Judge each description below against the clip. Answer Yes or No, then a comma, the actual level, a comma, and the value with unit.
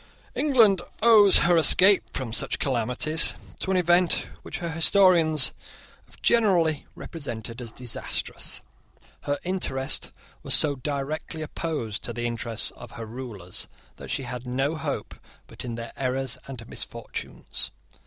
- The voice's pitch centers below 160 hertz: Yes, medium, 140 Hz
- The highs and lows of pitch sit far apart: Yes, wide, 6.0 semitones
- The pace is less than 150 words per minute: Yes, slow, 135 wpm